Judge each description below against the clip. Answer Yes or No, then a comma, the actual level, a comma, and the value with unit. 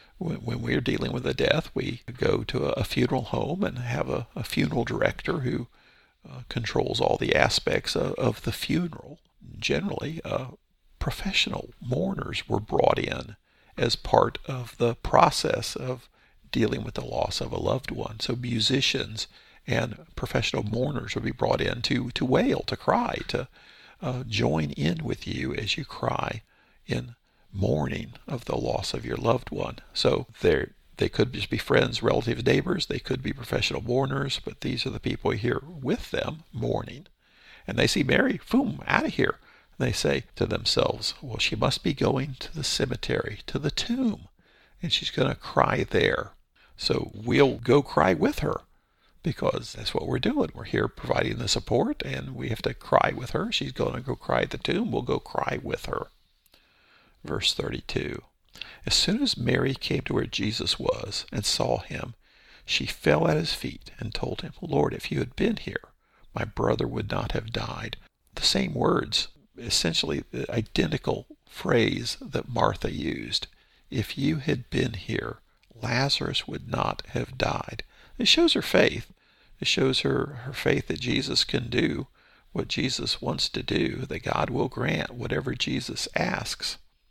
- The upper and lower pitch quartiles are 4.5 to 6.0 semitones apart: No, average, 4.1 semitones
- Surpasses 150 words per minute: Yes, average, 170 wpm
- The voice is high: No, low, 130 Hz